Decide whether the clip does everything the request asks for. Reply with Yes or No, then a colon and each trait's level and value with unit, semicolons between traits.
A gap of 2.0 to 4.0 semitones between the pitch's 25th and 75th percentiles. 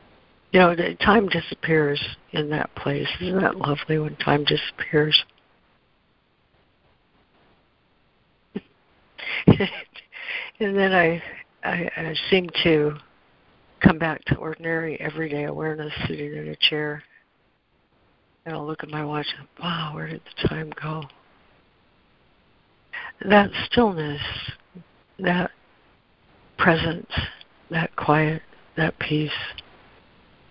Yes: average, 2.7 semitones